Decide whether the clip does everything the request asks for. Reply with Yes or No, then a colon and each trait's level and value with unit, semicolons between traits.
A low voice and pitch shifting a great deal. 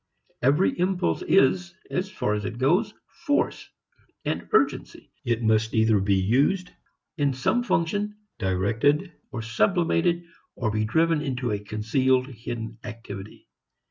Yes: low, 125 Hz; wide, 7.7 semitones